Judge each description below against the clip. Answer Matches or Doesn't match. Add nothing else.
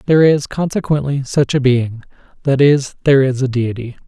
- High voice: Doesn't match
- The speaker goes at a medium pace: Matches